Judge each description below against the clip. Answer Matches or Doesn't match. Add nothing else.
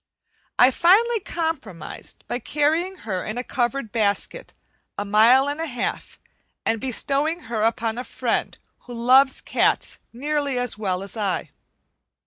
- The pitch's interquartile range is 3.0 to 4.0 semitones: Doesn't match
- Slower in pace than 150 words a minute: Matches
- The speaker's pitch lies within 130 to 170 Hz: Doesn't match